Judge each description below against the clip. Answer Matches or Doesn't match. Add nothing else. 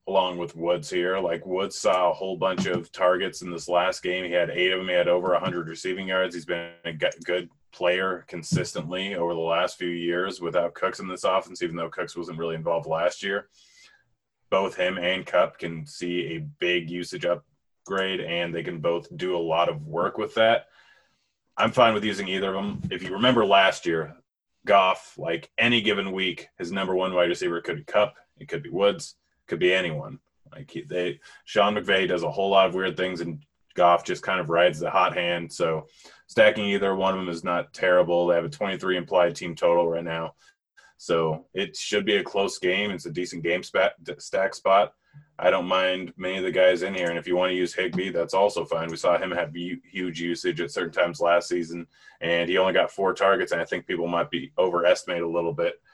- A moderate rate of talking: Doesn't match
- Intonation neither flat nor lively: Doesn't match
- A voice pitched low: Matches